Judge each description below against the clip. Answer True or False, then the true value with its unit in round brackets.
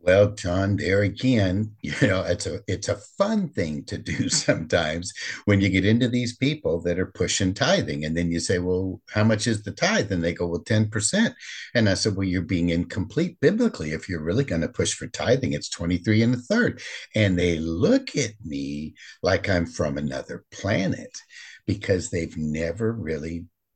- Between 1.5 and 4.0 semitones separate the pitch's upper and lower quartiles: False (4.5 semitones)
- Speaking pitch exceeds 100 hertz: False (95 Hz)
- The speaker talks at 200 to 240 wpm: False (190 wpm)